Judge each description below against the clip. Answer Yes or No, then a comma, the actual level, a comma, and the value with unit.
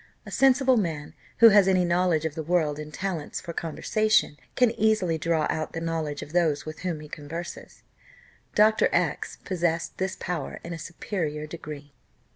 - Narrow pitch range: No, average, 3.6 semitones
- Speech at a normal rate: Yes, average, 170 wpm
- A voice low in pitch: No, medium, 170 Hz